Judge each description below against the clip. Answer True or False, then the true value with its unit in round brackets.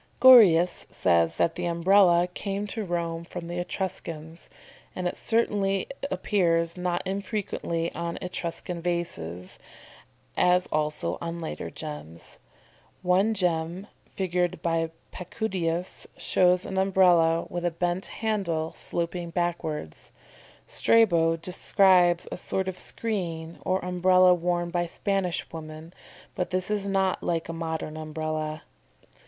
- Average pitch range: False (2.2 semitones)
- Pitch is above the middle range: False (175 Hz)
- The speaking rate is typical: False (125 wpm)